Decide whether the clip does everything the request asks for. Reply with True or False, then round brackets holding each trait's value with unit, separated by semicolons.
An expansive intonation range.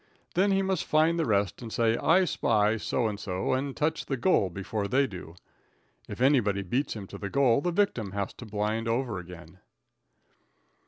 True (5.9 semitones)